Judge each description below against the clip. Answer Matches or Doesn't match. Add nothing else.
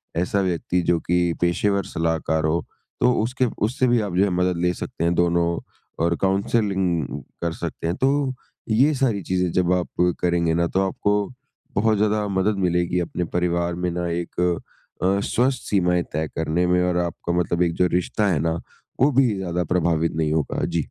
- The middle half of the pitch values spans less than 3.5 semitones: Matches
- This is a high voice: Doesn't match